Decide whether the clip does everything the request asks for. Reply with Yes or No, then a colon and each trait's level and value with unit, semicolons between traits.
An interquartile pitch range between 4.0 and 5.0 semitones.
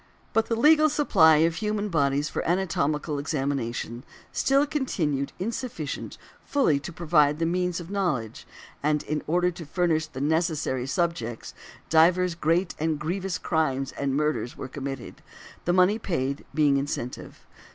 Yes: average, 4.3 semitones